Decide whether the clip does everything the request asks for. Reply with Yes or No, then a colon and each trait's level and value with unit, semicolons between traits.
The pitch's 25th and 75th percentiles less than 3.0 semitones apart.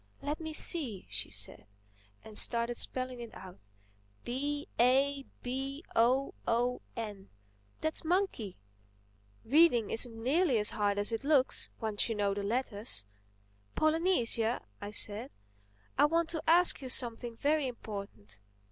No: average, 5.3 semitones